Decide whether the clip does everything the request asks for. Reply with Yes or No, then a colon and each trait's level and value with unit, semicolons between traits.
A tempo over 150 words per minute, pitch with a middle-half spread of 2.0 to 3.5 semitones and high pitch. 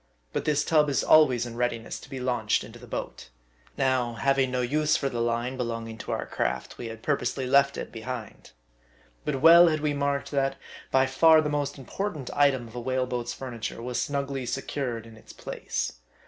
No: average, 190 wpm; average, 3.0 semitones; low, 130 Hz